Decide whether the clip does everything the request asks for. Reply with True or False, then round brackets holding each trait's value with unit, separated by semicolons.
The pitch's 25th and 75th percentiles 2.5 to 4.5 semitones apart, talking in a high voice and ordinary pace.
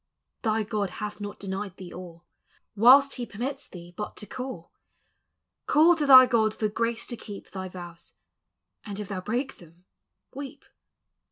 False (5.1 semitones; 210 Hz; 160 wpm)